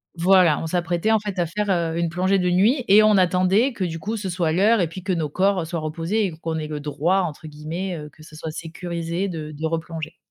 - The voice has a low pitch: No, medium, 175 Hz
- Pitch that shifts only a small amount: No, average, 3.0 semitones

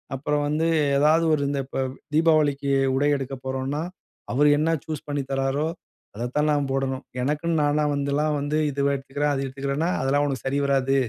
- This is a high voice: No, medium, 140 Hz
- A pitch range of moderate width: No, narrow, 1.7 semitones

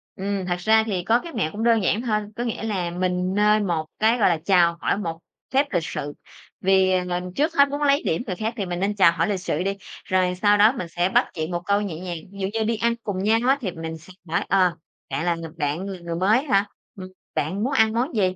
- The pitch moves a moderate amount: Yes, average, 3.7 semitones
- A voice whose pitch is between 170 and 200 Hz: Yes, high, 195 Hz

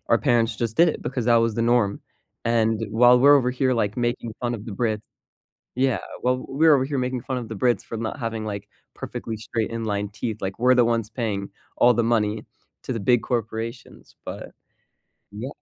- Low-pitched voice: Yes, low, 115 Hz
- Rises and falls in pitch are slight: Yes, narrow, 2.1 semitones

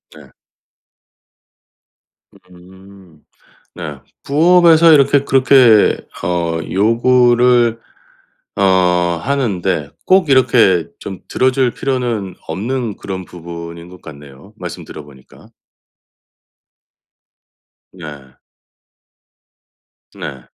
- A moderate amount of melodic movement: No, wide, 7.3 semitones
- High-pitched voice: No, low, 100 Hz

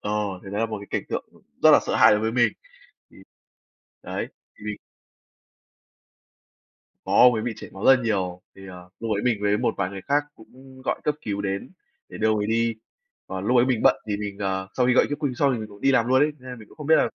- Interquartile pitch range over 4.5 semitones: No, average, 3.8 semitones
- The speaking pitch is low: Yes, low, 110 Hz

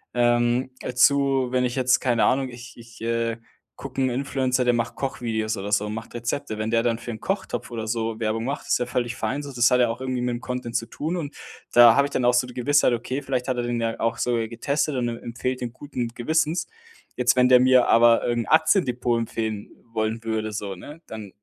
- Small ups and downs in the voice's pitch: Yes, narrow, 2.1 semitones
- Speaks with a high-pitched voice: No, low, 120 Hz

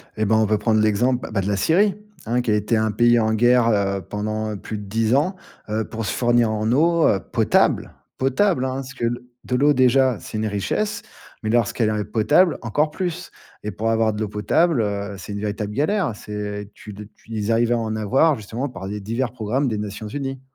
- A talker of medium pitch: No, low, 110 Hz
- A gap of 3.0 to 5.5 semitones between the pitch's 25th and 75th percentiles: Yes, average, 3.7 semitones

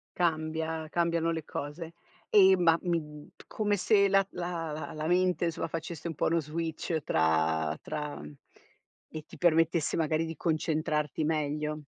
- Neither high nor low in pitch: Yes, medium, 160 Hz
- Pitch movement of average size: No, narrow, 2.0 semitones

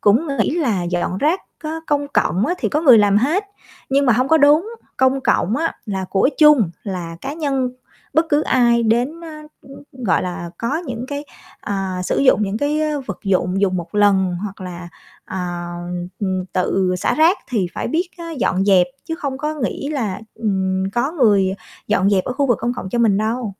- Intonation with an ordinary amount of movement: No, wide, 7.1 semitones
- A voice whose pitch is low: No, high, 230 Hz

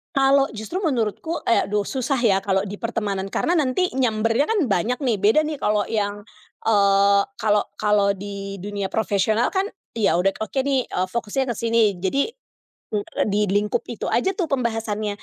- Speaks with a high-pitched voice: Yes, high, 215 Hz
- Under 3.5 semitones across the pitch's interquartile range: No, average, 4.2 semitones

